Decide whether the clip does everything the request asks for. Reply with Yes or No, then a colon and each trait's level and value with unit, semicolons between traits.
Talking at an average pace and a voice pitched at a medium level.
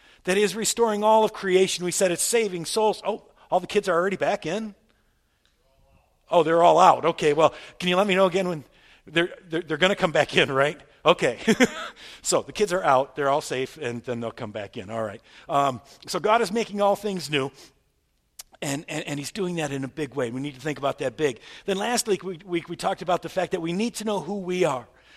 No: fast, 240 wpm; medium, 175 Hz